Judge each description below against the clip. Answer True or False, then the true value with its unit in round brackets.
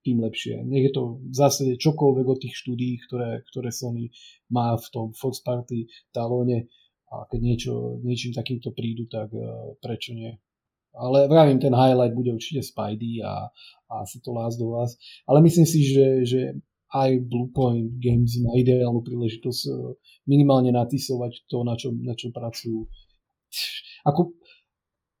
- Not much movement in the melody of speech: True (1.9 semitones)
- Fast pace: False (150 wpm)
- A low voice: True (120 Hz)